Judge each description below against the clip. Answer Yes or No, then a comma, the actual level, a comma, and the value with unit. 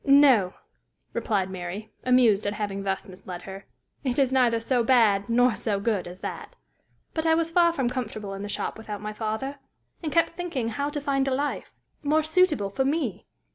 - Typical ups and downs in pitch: No, wide, 5.7 semitones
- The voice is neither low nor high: No, high, 235 Hz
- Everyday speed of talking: Yes, average, 190 wpm